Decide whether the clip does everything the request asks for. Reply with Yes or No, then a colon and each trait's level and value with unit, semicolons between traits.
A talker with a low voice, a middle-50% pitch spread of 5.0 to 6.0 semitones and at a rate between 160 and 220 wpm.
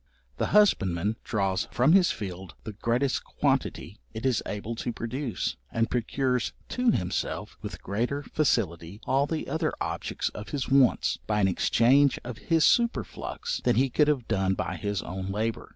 Yes: low, 115 Hz; wide, 5.5 semitones; average, 165 wpm